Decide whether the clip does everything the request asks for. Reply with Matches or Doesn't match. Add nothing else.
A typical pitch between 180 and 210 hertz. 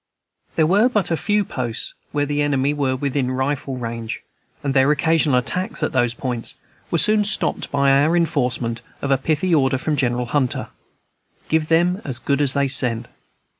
Doesn't match